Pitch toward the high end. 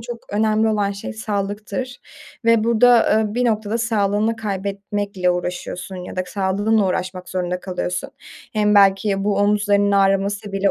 Yes: high, 205 Hz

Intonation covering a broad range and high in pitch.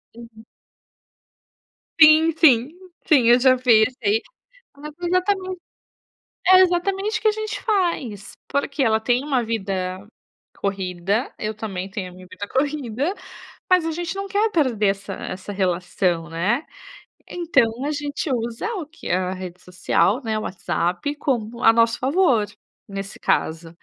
Yes: wide, 7.9 semitones; high, 235 Hz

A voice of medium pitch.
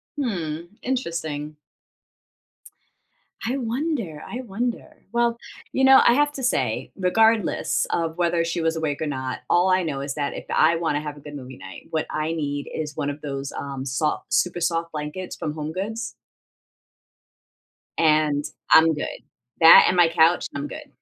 Yes: medium, 160 Hz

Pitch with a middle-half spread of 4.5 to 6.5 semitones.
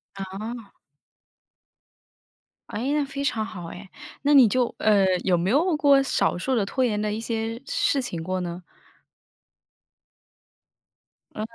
Yes: wide, 5.4 semitones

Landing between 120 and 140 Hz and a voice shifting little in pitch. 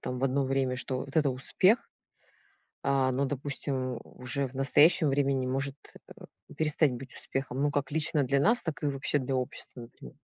Yes: low, 135 Hz; narrow, 1.8 semitones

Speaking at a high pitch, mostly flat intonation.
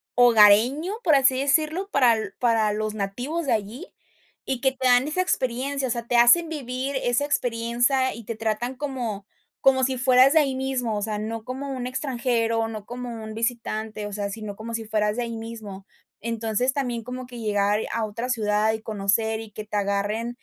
No: high, 235 Hz; average, 3.2 semitones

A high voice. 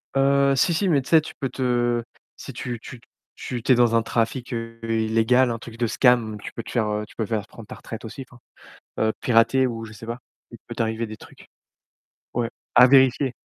No: low, 120 Hz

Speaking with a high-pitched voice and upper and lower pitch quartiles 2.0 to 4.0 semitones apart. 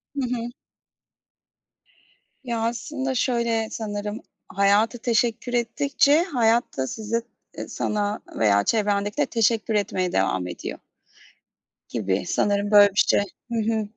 Yes: high, 220 Hz; narrow, 2.6 semitones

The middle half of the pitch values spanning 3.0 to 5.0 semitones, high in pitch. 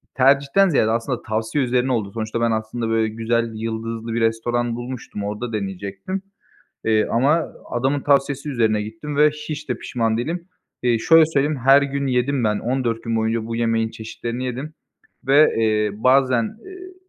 No: average, 3.7 semitones; low, 120 Hz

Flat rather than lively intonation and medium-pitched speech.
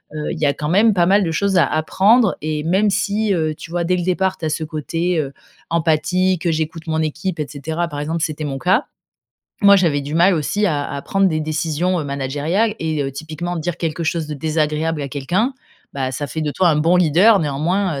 No: average, 3.3 semitones; medium, 160 Hz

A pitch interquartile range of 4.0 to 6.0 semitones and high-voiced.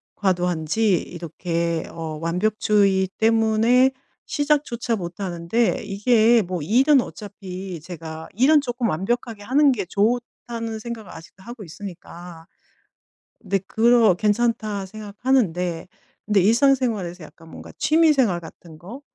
Yes: average, 5.2 semitones; high, 205 Hz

